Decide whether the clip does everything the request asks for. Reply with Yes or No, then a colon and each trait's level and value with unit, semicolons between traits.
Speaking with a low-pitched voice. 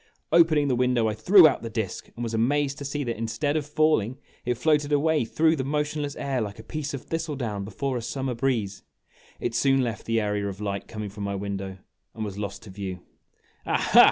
Yes: low, 120 Hz